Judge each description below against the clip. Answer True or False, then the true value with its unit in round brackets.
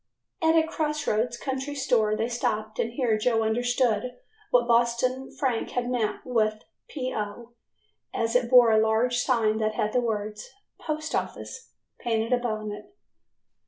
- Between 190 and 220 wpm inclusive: False (155 wpm)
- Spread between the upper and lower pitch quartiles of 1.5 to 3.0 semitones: True (2.5 semitones)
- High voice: True (235 Hz)